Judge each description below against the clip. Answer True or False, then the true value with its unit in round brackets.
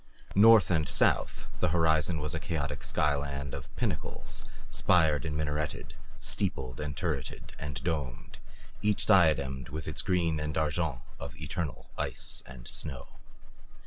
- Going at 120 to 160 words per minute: True (140 wpm)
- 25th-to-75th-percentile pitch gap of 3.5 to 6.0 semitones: False (2.5 semitones)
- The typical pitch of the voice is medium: False (75 Hz)